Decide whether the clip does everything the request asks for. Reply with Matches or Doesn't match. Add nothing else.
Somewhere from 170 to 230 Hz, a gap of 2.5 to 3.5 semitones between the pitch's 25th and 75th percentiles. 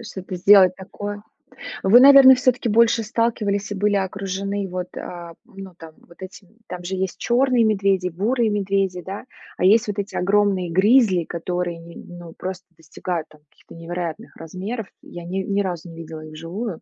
Matches